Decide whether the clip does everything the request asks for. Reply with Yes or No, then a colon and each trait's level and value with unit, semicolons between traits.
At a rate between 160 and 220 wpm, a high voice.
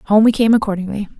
Yes: average, 200 wpm; high, 210 Hz